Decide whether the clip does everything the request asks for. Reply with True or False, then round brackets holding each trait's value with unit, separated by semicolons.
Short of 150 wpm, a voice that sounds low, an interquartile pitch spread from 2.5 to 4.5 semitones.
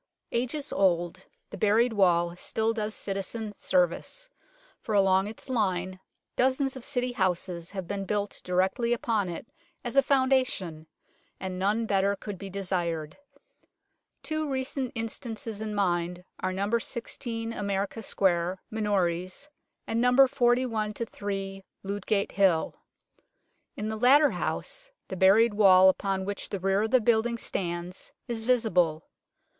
False (135 wpm; 205 Hz; 3.9 semitones)